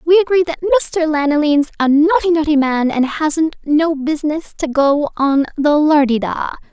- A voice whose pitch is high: Yes, very high, 305 Hz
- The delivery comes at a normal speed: Yes, average, 170 wpm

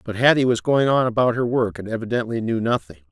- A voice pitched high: No, low, 120 Hz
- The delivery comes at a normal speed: No, fast, 230 wpm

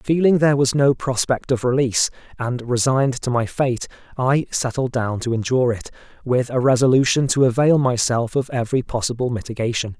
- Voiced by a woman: No, male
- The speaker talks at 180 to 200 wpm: No, average, 170 wpm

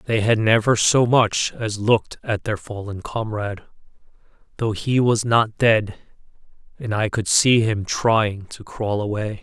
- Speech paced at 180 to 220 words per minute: No, average, 160 wpm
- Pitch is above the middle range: No, low, 110 Hz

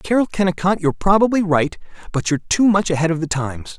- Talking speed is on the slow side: No, fast, 205 wpm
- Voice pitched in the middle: Yes, medium, 175 Hz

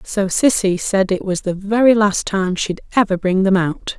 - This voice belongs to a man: No, female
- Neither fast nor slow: No, fast, 210 wpm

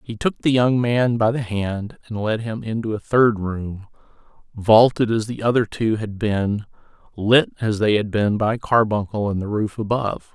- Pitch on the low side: Yes, low, 110 Hz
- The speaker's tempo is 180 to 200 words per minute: Yes, average, 190 wpm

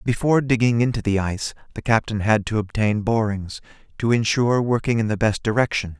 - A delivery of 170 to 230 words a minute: Yes, average, 180 wpm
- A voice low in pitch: Yes, low, 110 Hz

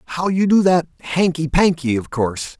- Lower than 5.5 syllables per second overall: Yes, 5.3 syllables/s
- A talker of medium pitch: Yes, medium, 160 Hz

